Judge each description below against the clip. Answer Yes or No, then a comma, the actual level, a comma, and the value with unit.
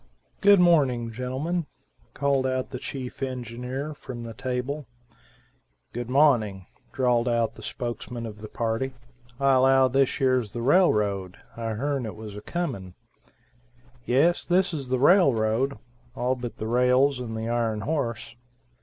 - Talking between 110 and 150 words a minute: Yes, average, 140 wpm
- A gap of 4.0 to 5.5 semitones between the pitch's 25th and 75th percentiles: No, average, 3.0 semitones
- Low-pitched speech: Yes, low, 125 Hz